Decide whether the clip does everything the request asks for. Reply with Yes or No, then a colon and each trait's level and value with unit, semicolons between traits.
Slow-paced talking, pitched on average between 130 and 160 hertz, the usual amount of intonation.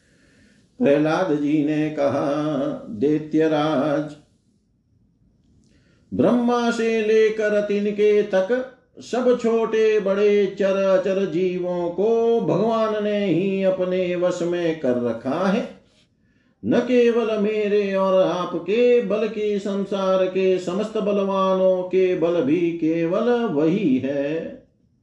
No: slow, 105 wpm; high, 190 Hz; average, 4.4 semitones